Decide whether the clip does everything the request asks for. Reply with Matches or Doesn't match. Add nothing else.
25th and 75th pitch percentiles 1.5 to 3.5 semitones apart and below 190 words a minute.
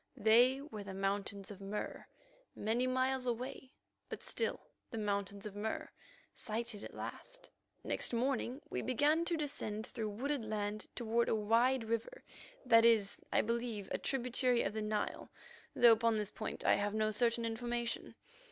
Matches